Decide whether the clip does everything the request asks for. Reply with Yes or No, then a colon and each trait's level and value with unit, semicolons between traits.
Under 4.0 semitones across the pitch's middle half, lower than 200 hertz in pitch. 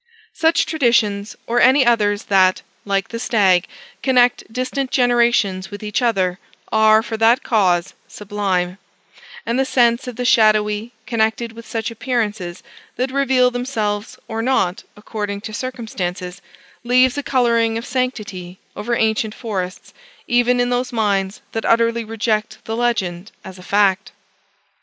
No: average, 3.2 semitones; high, 225 Hz